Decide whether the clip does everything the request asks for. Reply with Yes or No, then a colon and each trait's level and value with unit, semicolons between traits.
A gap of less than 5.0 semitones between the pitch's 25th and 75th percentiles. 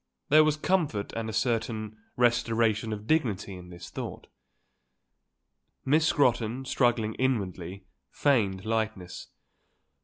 Yes: average, 4.0 semitones